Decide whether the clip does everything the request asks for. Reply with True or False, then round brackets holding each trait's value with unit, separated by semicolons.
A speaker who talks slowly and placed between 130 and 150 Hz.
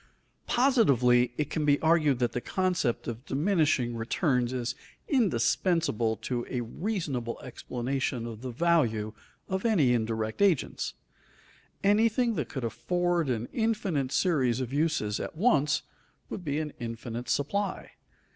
True (130 wpm; 140 Hz)